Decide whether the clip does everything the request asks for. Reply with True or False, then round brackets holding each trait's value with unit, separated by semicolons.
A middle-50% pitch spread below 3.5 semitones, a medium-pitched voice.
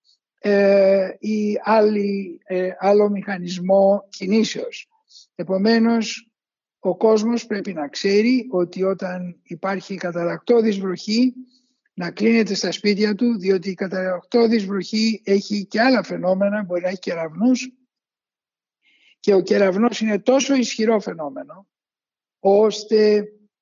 False (2.9 semitones; 205 Hz)